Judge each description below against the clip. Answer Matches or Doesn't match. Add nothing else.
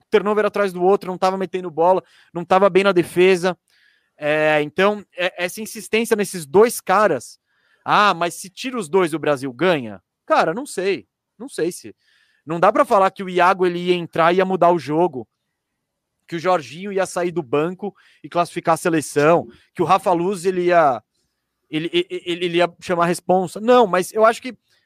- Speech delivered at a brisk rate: Matches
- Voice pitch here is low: Doesn't match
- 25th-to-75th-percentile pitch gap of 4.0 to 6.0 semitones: Doesn't match